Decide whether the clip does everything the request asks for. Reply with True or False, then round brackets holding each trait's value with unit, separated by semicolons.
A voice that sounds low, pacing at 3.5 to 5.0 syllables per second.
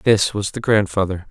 True (100 Hz; 4.8 syllables/s)